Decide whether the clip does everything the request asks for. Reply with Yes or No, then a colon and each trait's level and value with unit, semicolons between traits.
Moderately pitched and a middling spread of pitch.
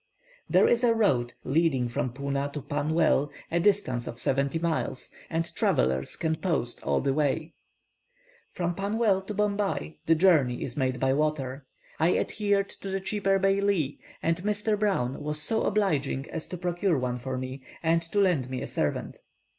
No: medium, 160 Hz; wide, 6.5 semitones